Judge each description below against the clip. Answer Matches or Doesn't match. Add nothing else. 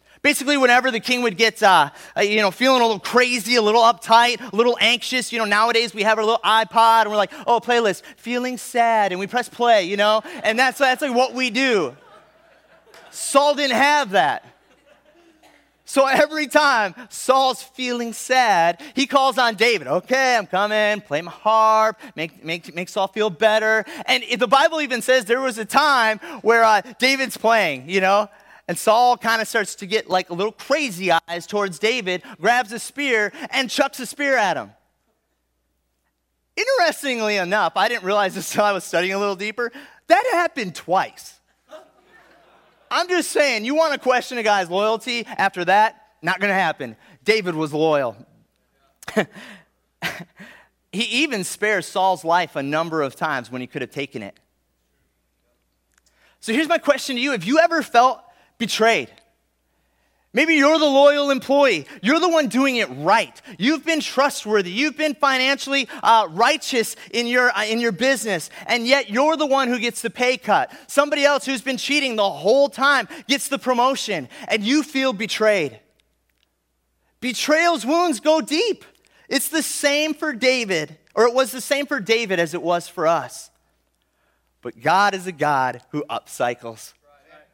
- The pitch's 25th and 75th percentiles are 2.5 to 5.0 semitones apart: Doesn't match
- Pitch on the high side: Matches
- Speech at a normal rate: Matches